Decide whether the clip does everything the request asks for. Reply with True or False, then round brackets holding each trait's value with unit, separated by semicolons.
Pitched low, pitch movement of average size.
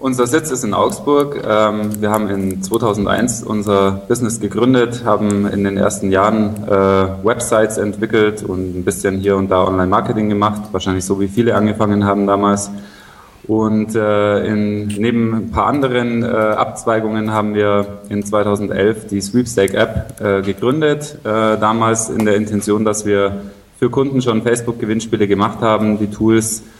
False (105 Hz; 1.8 semitones)